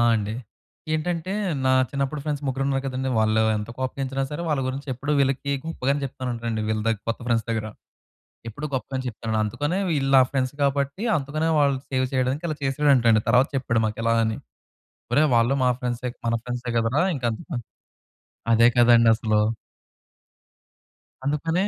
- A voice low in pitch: Yes, low, 130 Hz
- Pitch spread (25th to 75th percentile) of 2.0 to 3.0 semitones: No, average, 3.4 semitones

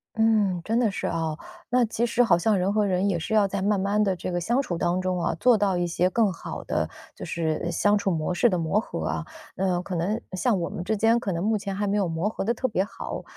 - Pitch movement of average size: Yes, average, 3.6 semitones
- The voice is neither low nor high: No, high, 195 Hz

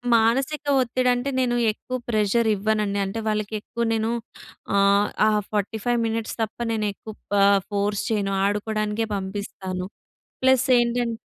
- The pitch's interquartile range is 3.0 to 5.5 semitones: No, narrow, 2.6 semitones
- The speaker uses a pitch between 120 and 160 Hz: No, high, 220 Hz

